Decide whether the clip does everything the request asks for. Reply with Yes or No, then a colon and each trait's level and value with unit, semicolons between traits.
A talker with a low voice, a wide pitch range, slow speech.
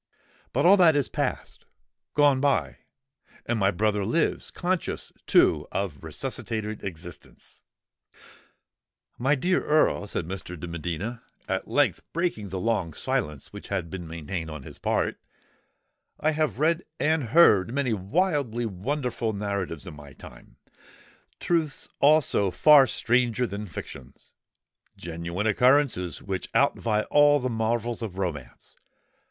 Yes: low, 110 Hz; wide, 7.8 semitones; slow, 120 wpm